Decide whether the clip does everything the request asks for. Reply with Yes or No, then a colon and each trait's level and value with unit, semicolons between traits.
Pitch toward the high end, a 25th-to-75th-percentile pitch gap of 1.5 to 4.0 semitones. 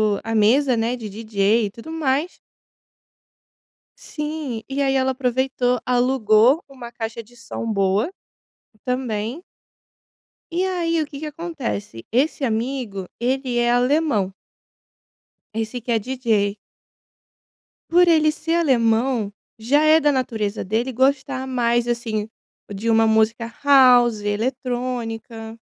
Yes: high, 245 Hz; average, 3.4 semitones